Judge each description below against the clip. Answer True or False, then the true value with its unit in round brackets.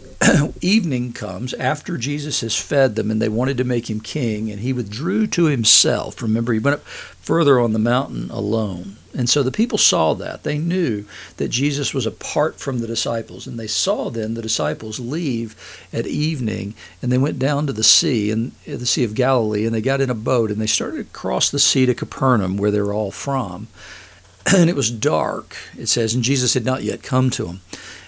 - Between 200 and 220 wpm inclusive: True (205 wpm)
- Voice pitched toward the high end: False (120 Hz)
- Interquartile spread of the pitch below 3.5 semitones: False (4.0 semitones)